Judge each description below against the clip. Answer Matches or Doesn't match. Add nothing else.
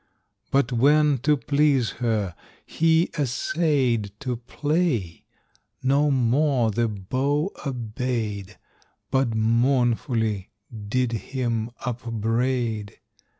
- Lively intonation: Doesn't match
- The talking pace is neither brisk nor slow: Doesn't match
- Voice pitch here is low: Matches